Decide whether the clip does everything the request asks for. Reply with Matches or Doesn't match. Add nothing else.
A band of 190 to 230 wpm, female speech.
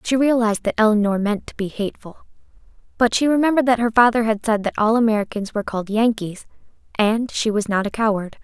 Matches